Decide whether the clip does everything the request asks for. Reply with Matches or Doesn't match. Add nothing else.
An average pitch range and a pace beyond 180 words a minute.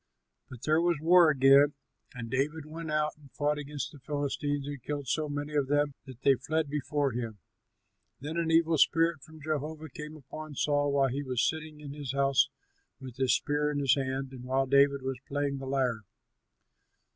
Doesn't match